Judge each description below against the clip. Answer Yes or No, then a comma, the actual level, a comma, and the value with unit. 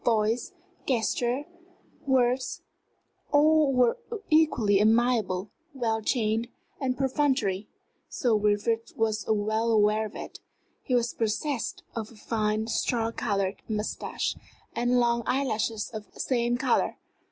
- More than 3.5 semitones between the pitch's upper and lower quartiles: No, average, 2.7 semitones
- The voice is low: No, high, 230 Hz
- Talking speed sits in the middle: No, slow, 120 wpm